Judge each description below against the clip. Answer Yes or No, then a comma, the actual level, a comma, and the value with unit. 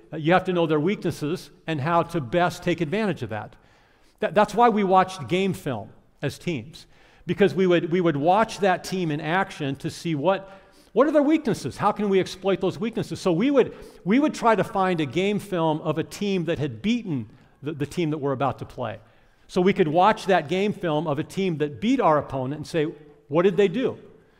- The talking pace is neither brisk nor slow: No, fast, 225 wpm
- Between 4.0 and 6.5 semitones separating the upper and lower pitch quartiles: Yes, average, 4.4 semitones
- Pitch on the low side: No, medium, 175 Hz